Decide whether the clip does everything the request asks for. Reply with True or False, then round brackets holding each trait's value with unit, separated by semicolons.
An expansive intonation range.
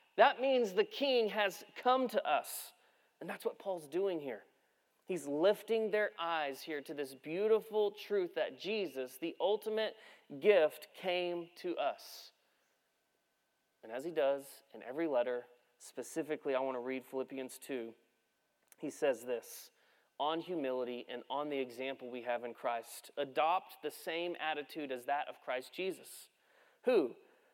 True (8.5 semitones)